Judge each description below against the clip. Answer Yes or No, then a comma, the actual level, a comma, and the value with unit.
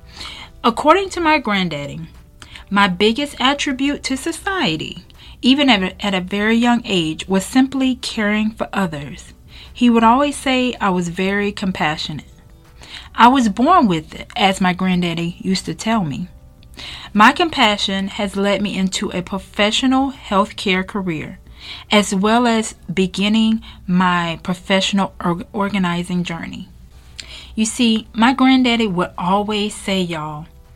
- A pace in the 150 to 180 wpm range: No, slow, 135 wpm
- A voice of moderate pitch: No, high, 200 Hz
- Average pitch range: Yes, average, 4.5 semitones